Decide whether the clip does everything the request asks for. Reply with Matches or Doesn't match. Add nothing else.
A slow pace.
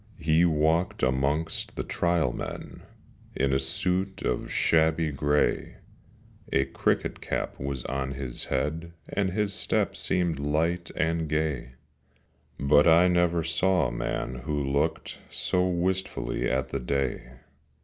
Matches